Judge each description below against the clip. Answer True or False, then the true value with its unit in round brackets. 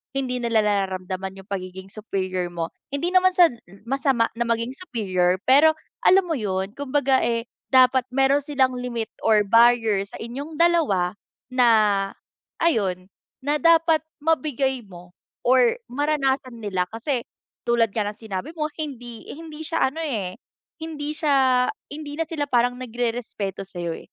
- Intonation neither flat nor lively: False (6.0 semitones)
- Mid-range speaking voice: False (245 Hz)